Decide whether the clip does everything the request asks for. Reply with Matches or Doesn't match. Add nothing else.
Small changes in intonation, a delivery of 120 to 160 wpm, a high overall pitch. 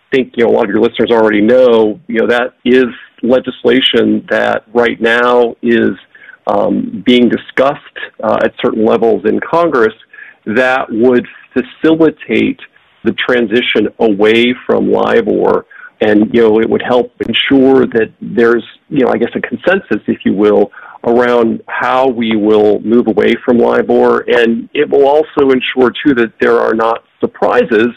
Doesn't match